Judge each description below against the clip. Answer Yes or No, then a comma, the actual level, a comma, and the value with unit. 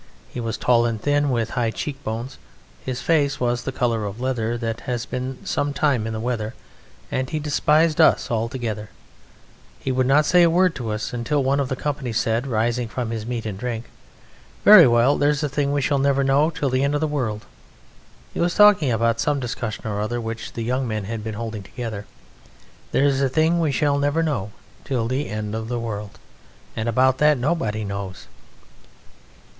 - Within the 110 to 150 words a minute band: No, average, 195 wpm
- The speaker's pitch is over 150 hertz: No, low, 125 Hz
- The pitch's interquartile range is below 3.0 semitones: No, average, 4.1 semitones